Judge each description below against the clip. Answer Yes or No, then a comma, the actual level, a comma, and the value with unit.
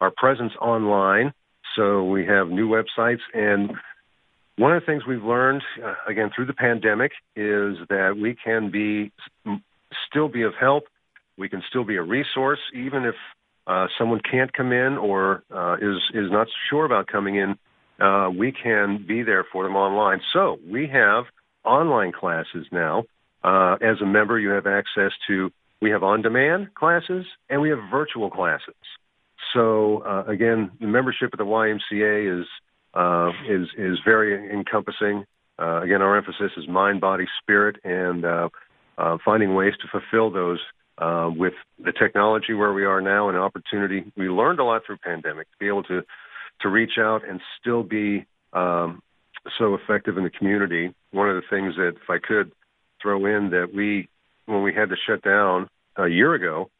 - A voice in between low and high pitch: No, low, 105 Hz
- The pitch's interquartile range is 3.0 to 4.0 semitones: No, narrow, 2.6 semitones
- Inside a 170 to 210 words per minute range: Yes, average, 175 wpm